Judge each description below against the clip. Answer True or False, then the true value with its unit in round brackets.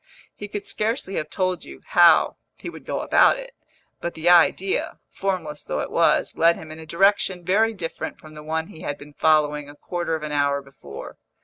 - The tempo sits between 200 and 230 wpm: True (205 wpm)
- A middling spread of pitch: True (4.0 semitones)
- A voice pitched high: False (160 Hz)